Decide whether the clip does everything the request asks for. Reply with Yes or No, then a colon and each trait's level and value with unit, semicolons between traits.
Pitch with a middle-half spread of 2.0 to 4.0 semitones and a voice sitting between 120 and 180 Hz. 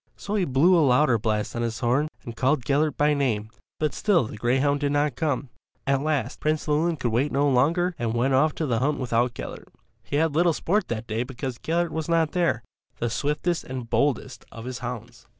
No: average, 4.4 semitones; medium, 140 Hz